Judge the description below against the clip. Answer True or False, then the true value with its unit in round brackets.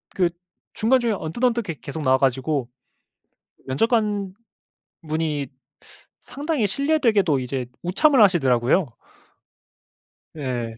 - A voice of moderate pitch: True (180 Hz)